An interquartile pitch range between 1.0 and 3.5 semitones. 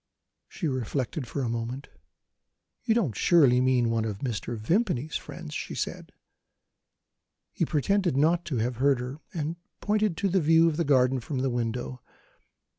No: average, 5.3 semitones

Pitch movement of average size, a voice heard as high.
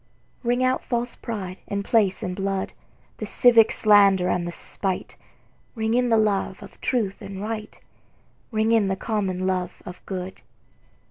Yes: average, 3.1 semitones; high, 200 Hz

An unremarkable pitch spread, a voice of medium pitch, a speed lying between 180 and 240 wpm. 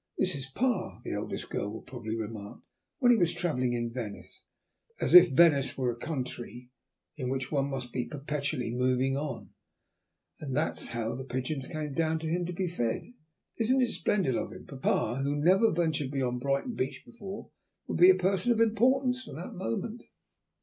No: wide, 6.4 semitones; medium, 145 Hz; average, 185 wpm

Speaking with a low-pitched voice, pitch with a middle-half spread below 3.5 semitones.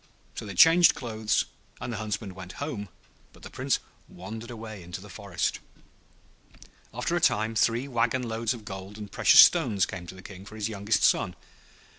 Yes: low, 105 Hz; average, 2.9 semitones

